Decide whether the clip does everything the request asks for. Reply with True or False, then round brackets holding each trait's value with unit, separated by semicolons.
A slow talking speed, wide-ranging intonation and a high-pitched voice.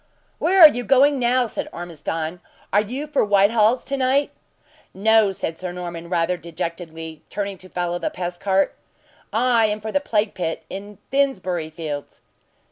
False (160 wpm; 5.8 semitones; 195 Hz)